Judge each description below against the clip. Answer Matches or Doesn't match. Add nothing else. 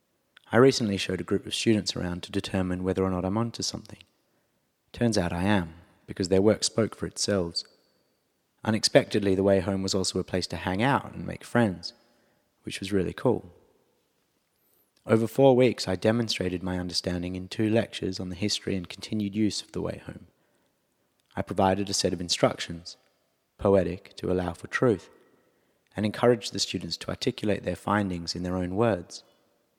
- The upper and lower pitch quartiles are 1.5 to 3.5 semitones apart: Matches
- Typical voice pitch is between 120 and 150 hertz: Doesn't match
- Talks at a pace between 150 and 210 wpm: Matches